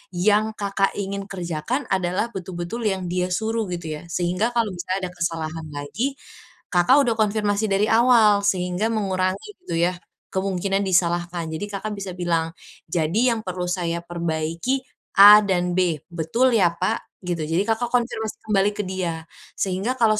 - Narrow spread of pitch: No, average, 3.4 semitones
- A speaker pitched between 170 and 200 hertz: Yes, high, 190 Hz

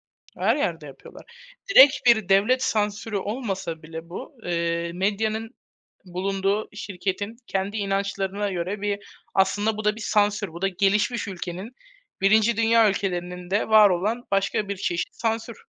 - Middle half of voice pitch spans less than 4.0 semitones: Yes, average, 2.7 semitones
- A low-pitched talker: No, high, 200 Hz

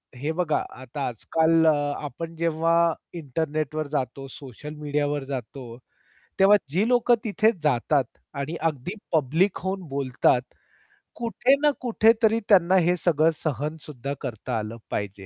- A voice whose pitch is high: No, medium, 155 Hz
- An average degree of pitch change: Yes, average, 4.1 semitones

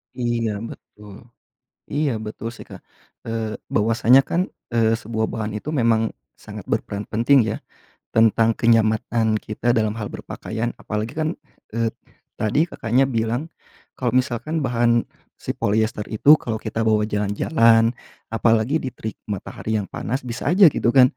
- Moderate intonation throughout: No, narrow, 1.9 semitones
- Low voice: Yes, low, 115 Hz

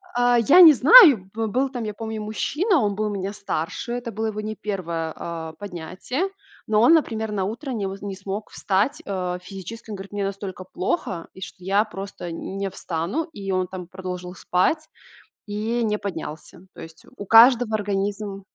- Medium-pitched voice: No, high, 205 Hz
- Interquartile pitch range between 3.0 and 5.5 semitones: Yes, average, 3.3 semitones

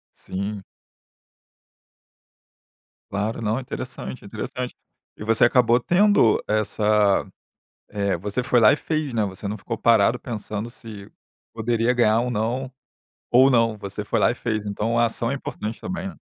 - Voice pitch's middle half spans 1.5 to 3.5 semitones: Yes, narrow, 2.6 semitones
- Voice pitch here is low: Yes, low, 115 Hz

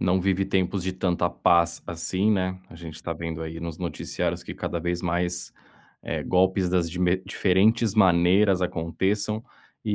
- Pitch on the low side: Yes, very low, 90 Hz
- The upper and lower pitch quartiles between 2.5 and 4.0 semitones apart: No, narrow, 2.0 semitones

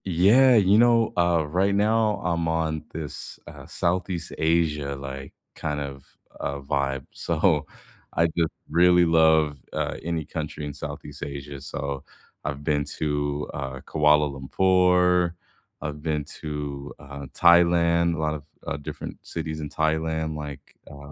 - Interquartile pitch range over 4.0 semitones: No, average, 3.0 semitones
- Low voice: Yes, very low, 80 Hz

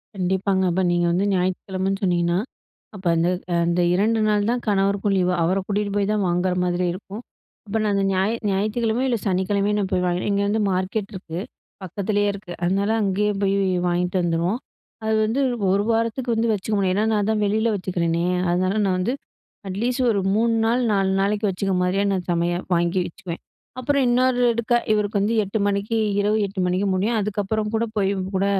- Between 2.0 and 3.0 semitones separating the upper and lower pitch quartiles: Yes, narrow, 2.6 semitones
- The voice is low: No, high, 200 Hz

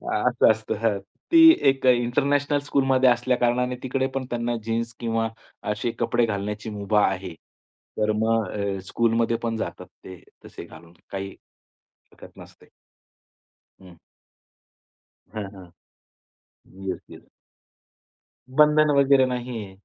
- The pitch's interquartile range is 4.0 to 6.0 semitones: No, average, 3.6 semitones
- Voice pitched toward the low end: Yes, low, 115 Hz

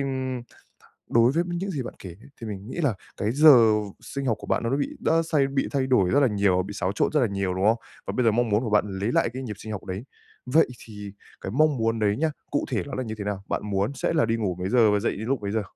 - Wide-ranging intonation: No, average, 4.9 semitones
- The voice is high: No, low, 115 Hz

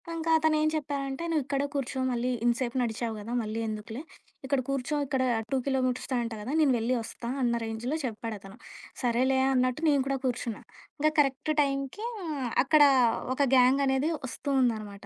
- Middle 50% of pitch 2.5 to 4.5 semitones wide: Yes, average, 2.9 semitones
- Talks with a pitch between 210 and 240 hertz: No, very high, 260 Hz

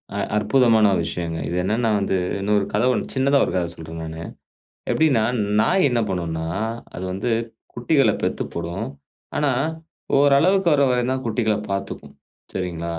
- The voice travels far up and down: Yes, wide, 6.9 semitones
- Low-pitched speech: Yes, low, 110 Hz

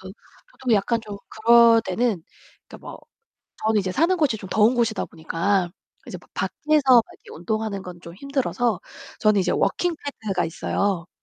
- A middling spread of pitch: Yes, average, 4.2 semitones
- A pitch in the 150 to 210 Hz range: No, high, 220 Hz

